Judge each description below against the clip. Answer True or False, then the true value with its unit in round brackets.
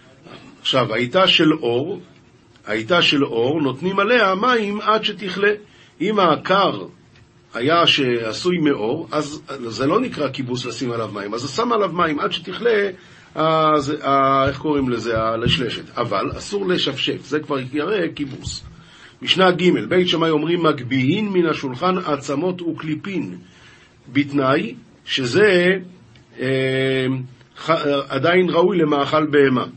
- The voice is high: False (150 Hz)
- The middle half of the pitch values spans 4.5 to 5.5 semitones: True (5.0 semitones)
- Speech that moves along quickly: False (125 wpm)